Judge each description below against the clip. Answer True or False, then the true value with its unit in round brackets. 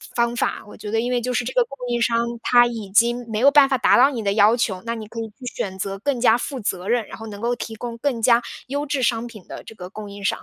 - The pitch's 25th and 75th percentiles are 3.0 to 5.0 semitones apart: False (2.5 semitones)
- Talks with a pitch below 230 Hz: False (235 Hz)